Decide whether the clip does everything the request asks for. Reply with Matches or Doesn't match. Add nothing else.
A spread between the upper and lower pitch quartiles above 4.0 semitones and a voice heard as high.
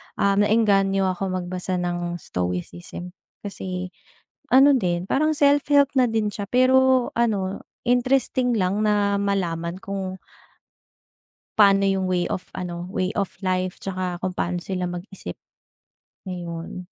Doesn't match